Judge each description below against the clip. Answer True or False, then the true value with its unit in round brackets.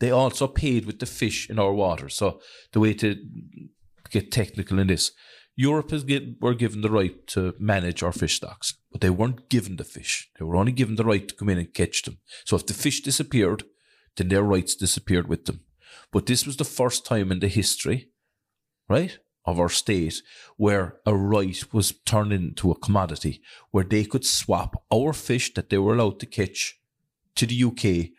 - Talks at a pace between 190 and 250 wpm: True (200 wpm)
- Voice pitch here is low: True (105 Hz)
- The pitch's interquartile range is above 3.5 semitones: True (4.5 semitones)